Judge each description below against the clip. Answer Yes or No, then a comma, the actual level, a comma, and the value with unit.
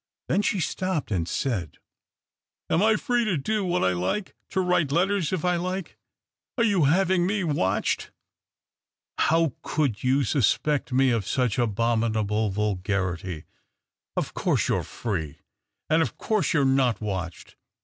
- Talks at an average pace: Yes, average, 170 wpm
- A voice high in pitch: No, low, 135 Hz